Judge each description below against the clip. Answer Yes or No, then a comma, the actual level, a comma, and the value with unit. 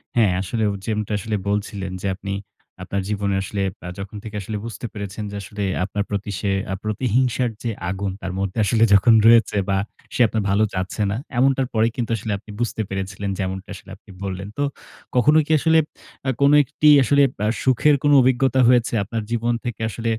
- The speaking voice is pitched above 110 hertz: No, low, 105 Hz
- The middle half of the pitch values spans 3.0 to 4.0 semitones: Yes, average, 3.3 semitones